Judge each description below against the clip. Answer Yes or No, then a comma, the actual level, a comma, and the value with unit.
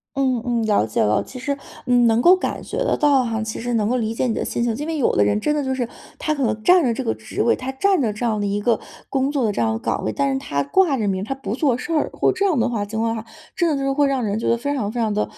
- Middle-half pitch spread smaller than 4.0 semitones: No, average, 4.4 semitones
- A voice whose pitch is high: Yes, high, 235 Hz